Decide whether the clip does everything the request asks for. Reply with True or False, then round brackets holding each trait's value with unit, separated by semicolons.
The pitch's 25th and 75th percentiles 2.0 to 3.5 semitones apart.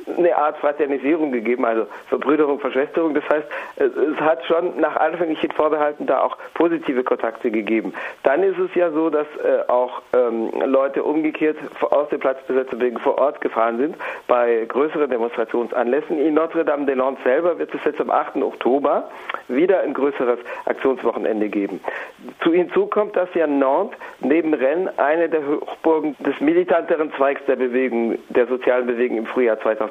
False (4.4 semitones)